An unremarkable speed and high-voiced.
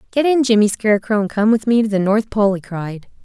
No: fast, 260 wpm; high, 215 Hz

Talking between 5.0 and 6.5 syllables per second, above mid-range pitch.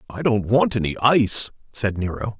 No: 5.2 syllables/s; low, 110 Hz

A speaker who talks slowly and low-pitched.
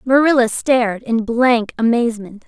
No: slow, 120 wpm; high, 235 Hz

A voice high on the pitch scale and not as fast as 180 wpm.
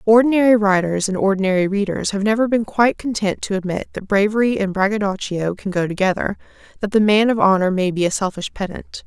No: high, 200 Hz; average, 190 wpm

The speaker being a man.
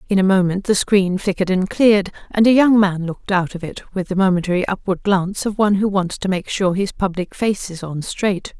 No: female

